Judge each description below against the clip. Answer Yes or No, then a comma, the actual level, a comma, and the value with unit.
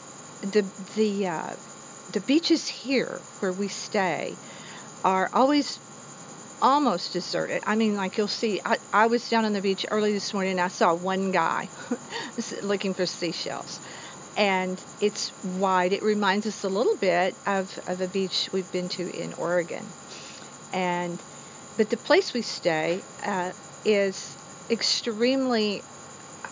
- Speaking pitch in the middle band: No, high, 195 Hz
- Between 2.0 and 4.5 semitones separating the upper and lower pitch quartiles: Yes, average, 3.3 semitones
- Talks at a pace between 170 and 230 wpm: No, average, 145 wpm